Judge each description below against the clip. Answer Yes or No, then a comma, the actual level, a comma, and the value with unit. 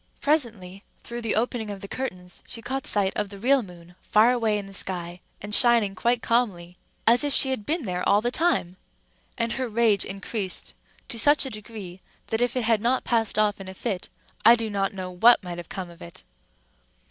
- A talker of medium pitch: No, high, 215 Hz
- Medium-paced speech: No, fast, 210 wpm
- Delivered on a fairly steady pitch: No, average, 3.9 semitones